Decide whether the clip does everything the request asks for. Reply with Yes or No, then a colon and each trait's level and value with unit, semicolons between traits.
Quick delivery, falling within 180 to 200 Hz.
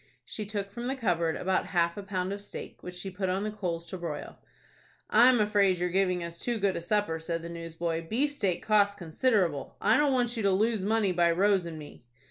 Yes: fast, 220 wpm; high, 190 Hz